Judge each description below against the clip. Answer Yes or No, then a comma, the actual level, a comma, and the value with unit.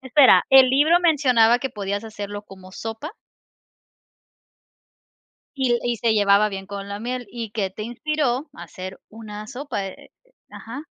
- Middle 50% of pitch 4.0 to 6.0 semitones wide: Yes, average, 4.5 semitones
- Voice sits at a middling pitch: No, high, 225 Hz